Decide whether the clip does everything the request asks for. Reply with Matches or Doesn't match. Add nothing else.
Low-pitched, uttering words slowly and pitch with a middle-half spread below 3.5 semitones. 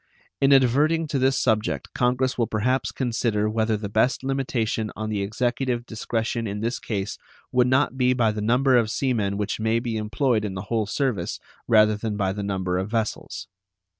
Doesn't match